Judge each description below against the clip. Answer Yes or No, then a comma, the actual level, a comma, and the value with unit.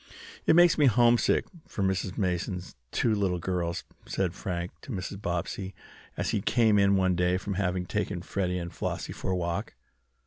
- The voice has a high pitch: No, very low, 95 Hz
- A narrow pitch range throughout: Yes, narrow, 2.3 semitones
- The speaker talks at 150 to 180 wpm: Yes, average, 175 wpm